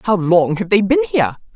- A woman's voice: Yes, female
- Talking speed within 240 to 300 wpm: No, fast, 230 wpm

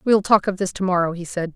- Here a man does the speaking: No, female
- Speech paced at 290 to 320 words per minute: Yes, fast, 310 wpm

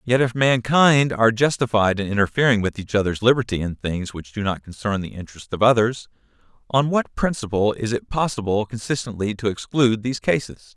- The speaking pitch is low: Yes, low, 115 Hz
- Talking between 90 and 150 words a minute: No, average, 180 wpm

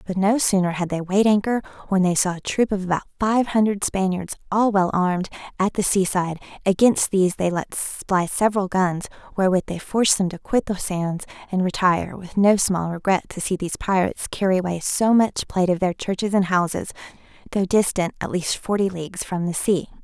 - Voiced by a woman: Yes, female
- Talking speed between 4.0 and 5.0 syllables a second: No, 5.6 syllables/s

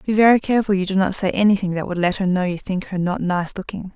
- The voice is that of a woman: Yes, female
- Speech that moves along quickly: Yes, fast, 290 wpm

